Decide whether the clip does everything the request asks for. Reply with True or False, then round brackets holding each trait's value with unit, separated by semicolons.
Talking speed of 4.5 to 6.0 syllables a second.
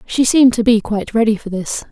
False (6.2 syllables/s)